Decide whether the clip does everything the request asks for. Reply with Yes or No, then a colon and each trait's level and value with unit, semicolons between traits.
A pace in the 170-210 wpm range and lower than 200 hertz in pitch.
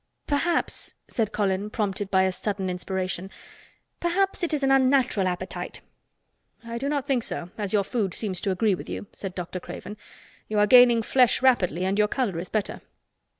No: average, 180 wpm; high, 210 Hz